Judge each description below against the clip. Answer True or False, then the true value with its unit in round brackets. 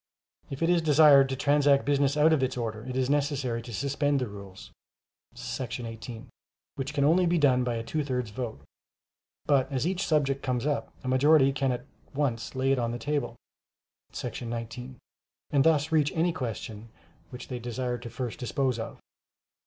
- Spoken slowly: False (185 wpm)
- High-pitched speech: False (130 Hz)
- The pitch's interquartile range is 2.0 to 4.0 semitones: True (3.1 semitones)